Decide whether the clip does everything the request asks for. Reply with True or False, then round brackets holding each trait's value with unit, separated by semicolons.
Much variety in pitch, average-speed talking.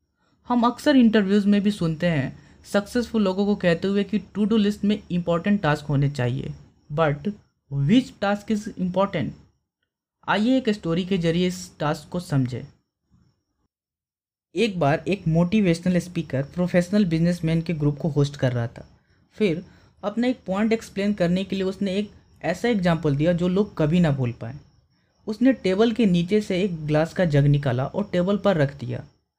True (5.7 semitones; 170 wpm)